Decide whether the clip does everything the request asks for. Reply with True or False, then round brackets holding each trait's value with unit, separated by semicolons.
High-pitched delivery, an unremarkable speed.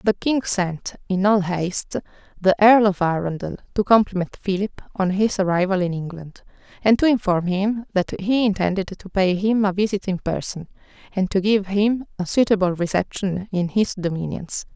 True (195 Hz; 170 wpm)